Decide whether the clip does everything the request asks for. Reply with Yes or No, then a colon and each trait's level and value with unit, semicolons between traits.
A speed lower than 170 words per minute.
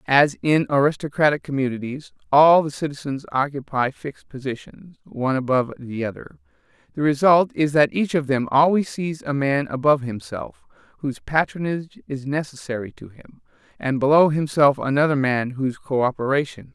Yes: average, 155 wpm